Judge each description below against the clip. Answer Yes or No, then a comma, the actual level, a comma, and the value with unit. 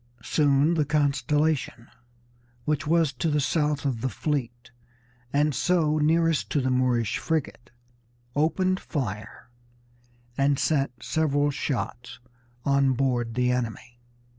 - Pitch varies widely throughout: No, average, 3.5 semitones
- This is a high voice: No, medium, 140 Hz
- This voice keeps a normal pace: No, slow, 115 wpm